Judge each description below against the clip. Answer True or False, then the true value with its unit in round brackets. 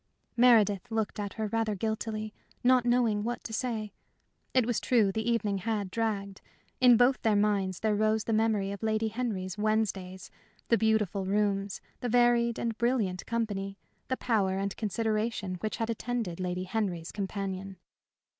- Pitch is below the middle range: False (215 Hz)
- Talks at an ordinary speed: True (155 wpm)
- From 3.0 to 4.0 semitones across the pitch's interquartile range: False (2.6 semitones)